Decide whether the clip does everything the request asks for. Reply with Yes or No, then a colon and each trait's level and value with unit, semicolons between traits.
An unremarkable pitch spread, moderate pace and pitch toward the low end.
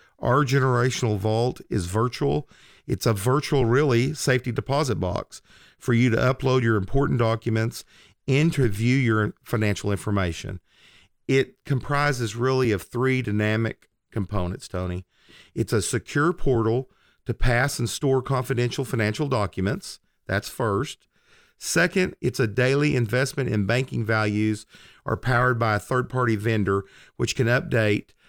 No: average, 3.5 semitones; slow, 130 wpm; low, 120 Hz